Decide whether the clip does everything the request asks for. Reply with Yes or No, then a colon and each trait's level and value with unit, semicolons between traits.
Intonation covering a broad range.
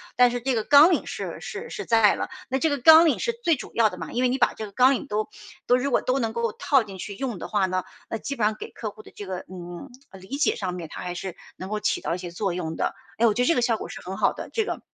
Yes: wide, 5.7 semitones